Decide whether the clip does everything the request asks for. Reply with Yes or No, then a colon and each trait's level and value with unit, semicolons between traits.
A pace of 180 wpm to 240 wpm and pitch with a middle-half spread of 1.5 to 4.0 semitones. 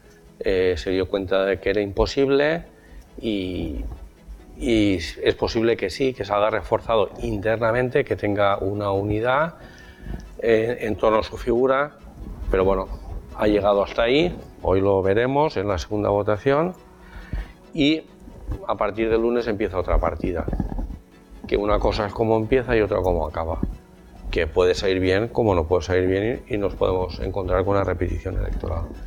No: average, 160 wpm; average, 3.5 semitones